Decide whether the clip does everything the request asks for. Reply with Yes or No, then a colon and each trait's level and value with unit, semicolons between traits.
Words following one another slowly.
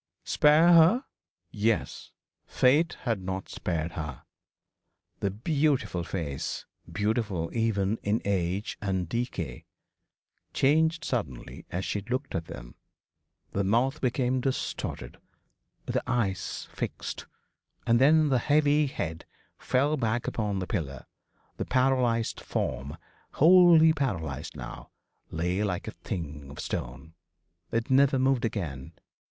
Yes: slow, 115 wpm